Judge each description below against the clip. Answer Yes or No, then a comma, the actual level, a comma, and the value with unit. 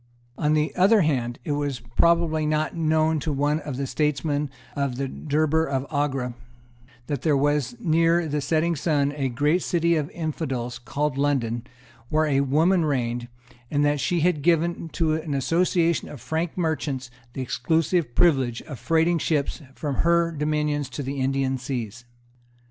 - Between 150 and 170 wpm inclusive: Yes, average, 160 wpm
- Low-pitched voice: No, medium, 150 Hz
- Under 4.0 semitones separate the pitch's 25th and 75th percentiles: Yes, average, 2.9 semitones